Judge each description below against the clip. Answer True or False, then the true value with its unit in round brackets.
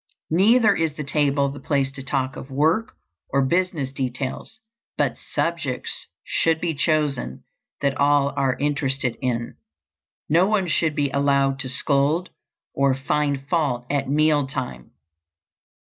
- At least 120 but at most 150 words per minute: True (135 wpm)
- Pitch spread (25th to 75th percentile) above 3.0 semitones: False (2.7 semitones)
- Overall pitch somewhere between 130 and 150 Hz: True (140 Hz)